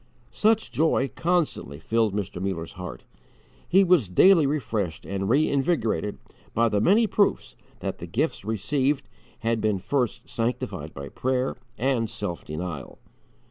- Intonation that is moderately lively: No, wide, 7.0 semitones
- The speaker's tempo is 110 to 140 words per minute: Yes, slow, 135 wpm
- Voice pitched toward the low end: Yes, low, 115 Hz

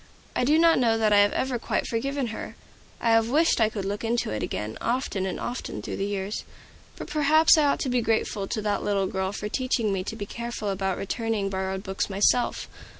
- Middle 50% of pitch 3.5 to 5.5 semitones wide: Yes, average, 3.9 semitones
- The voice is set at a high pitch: Yes, high, 220 Hz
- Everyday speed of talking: No, fast, 220 wpm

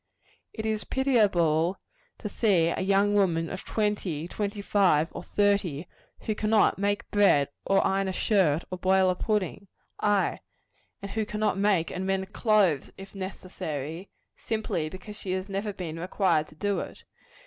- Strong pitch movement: No, average, 2.9 semitones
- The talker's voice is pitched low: No, high, 195 Hz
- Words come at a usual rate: Yes, average, 160 wpm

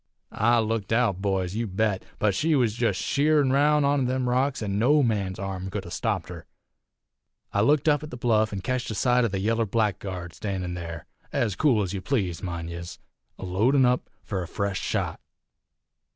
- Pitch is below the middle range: Yes, low, 110 Hz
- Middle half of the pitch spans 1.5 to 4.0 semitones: No, average, 4.9 semitones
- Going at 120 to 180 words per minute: No, average, 195 wpm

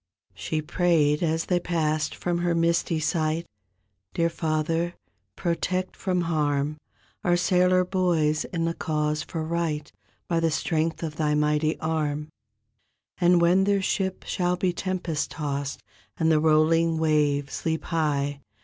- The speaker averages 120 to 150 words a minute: Yes, average, 140 wpm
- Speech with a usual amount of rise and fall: No, narrow, 2.3 semitones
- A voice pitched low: No, medium, 160 Hz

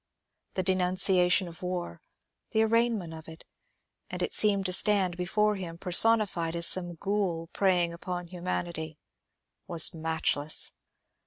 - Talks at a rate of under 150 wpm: Yes, average, 140 wpm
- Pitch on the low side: No, medium, 180 Hz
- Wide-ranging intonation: No, narrow, 2.5 semitones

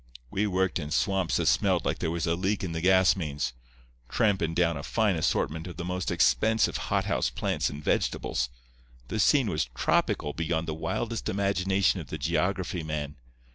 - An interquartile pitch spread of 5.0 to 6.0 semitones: No, average, 3.3 semitones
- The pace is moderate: Yes, average, 175 wpm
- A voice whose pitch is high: No, very low, 85 Hz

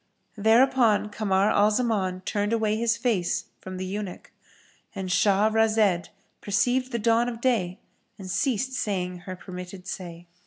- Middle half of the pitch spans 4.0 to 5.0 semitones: No, average, 3.6 semitones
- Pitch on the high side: Yes, high, 210 Hz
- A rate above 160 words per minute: No, average, 140 wpm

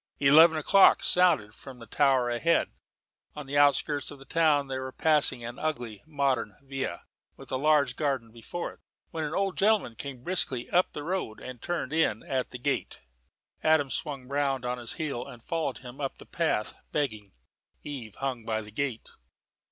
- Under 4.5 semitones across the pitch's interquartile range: Yes, average, 4.0 semitones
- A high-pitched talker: No, medium, 140 Hz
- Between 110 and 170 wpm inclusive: No, average, 180 wpm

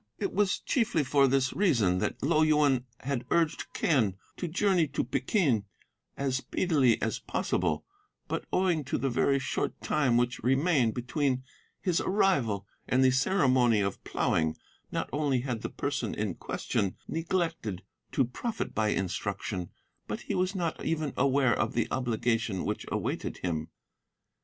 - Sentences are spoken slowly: No, average, 150 wpm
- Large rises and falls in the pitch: Yes, wide, 5.7 semitones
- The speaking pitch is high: No, low, 135 Hz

